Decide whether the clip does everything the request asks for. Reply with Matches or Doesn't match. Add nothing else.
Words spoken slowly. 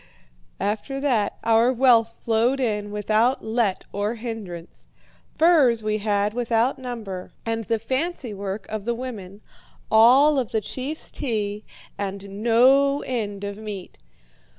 Matches